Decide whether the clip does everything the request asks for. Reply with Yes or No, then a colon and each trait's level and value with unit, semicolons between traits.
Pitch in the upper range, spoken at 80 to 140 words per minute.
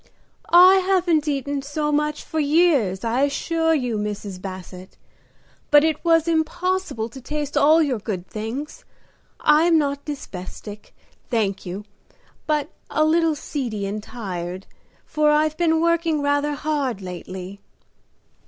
Yes: very high, 285 Hz; slow, 135 wpm